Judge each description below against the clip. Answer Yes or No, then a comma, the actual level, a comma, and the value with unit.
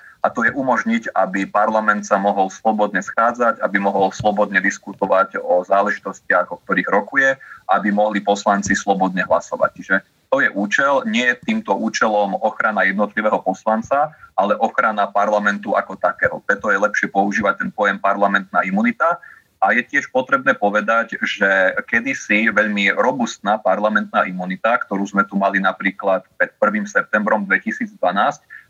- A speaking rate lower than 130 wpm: No, average, 140 wpm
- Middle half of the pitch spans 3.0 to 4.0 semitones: No, narrow, 2.6 semitones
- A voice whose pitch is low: Yes, low, 105 Hz